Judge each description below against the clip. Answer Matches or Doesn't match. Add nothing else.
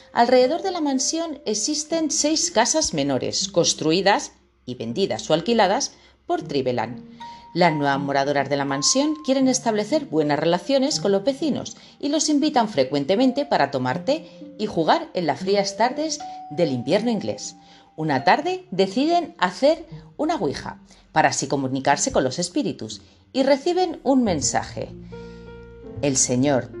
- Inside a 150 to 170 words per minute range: Doesn't match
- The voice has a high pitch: Matches